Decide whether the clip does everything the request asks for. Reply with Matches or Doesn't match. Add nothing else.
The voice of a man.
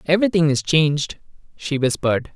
Matches